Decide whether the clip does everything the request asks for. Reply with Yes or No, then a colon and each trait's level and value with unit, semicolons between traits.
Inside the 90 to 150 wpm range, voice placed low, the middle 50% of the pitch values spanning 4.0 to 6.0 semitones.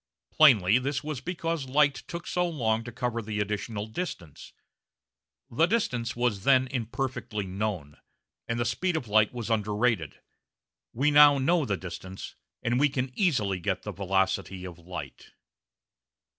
Yes: average, 145 wpm; low, 115 Hz; wide, 5.6 semitones